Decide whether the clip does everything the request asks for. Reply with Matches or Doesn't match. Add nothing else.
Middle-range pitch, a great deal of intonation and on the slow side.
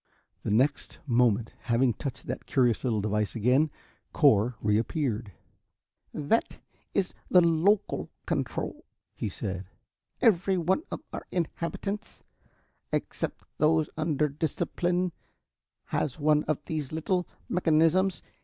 Matches